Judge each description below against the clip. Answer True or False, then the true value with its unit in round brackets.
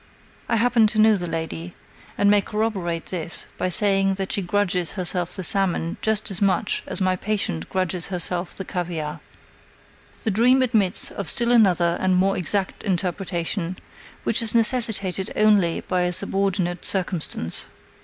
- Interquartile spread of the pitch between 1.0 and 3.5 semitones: True (2.9 semitones)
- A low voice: False (190 Hz)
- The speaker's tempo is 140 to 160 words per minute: True (155 wpm)